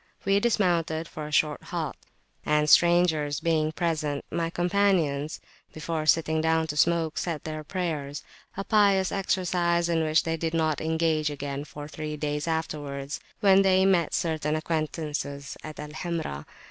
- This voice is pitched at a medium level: Yes, medium, 160 Hz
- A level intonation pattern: Yes, narrow, 2.2 semitones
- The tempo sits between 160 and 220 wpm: No, average, 145 wpm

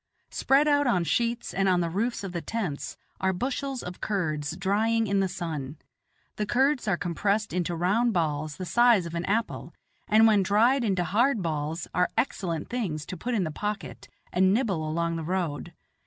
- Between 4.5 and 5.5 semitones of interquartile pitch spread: Yes, average, 5.2 semitones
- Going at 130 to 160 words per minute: No, average, 185 wpm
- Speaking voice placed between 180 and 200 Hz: Yes, high, 190 Hz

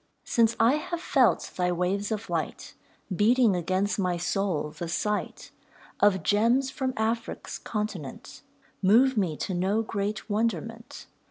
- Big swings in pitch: No, average, 3.7 semitones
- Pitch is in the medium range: No, high, 210 Hz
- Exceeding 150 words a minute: No, slow, 135 wpm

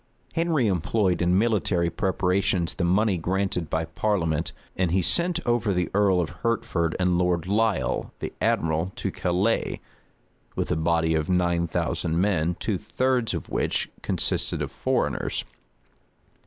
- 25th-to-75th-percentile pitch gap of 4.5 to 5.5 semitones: No, average, 3.6 semitones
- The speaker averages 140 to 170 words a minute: Yes, average, 145 wpm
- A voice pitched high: No, very low, 90 Hz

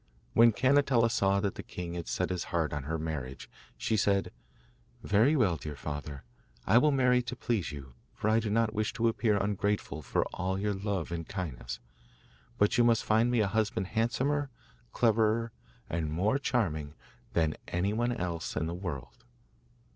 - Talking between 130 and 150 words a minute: No, average, 170 wpm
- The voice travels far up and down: Yes, wide, 5.7 semitones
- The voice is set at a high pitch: No, low, 100 Hz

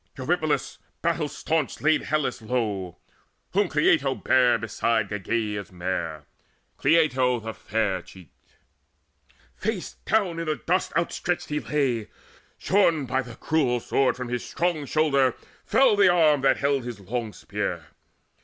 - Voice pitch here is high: No, low, 130 Hz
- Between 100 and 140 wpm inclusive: Yes, slow, 135 wpm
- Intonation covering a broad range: Yes, wide, 6.1 semitones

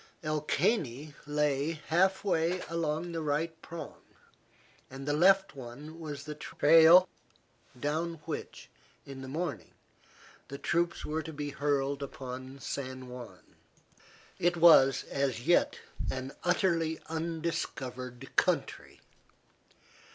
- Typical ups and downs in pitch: Yes, average, 3.6 semitones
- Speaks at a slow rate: Yes, slow, 110 wpm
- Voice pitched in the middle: Yes, medium, 150 Hz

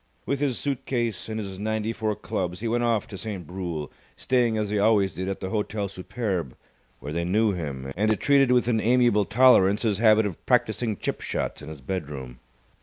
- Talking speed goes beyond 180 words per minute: Yes, average, 200 wpm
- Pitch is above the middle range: No, low, 105 Hz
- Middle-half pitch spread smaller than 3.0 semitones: No, average, 4.0 semitones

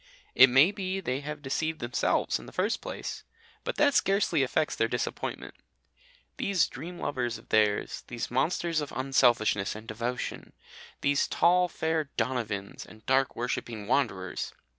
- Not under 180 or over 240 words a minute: No, average, 145 wpm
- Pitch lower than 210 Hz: Yes, low, 135 Hz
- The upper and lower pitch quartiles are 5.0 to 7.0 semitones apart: Yes, wide, 5.6 semitones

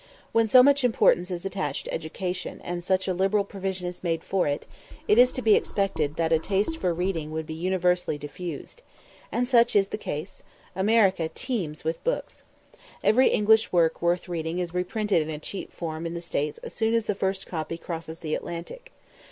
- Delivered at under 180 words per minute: No, average, 195 wpm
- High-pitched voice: No, medium, 180 Hz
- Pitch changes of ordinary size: Yes, average, 4.0 semitones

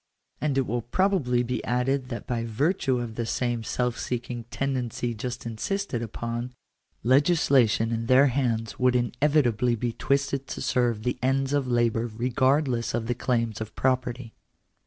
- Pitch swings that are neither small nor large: No, narrow, 2.2 semitones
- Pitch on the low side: Yes, low, 125 Hz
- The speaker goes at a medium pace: Yes, average, 155 wpm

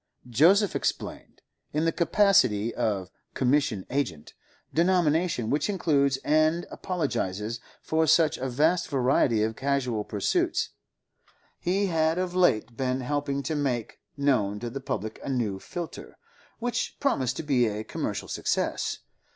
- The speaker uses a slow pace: Yes, slow, 125 wpm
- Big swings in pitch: Yes, wide, 5.7 semitones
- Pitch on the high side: No, medium, 140 Hz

